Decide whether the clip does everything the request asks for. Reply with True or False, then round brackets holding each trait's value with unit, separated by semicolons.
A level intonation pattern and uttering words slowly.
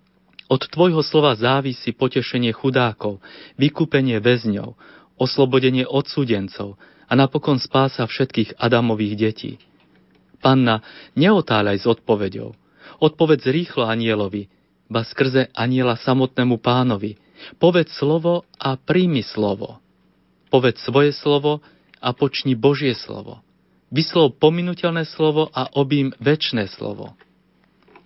False (4.4 semitones; 100 wpm)